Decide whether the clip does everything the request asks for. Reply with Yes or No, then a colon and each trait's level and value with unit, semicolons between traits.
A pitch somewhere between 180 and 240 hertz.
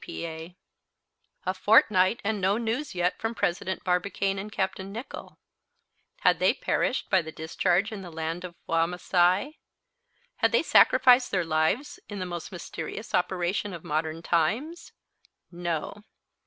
Yes: medium, 185 Hz